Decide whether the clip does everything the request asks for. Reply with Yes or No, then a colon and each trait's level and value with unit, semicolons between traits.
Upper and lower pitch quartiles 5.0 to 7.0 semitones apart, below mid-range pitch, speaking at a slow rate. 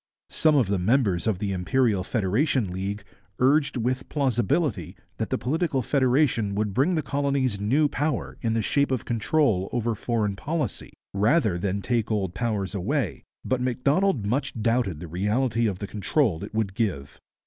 No: average, 5.3 semitones; low, 115 Hz; average, 160 wpm